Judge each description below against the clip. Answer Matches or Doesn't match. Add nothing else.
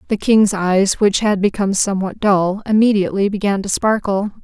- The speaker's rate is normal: Matches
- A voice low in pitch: Doesn't match